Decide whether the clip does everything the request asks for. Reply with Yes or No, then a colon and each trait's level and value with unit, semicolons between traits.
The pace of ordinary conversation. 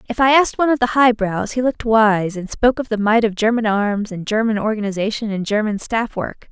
No: fast, 230 wpm